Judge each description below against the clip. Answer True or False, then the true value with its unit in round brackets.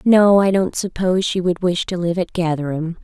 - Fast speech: True (220 wpm)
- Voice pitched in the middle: True (180 Hz)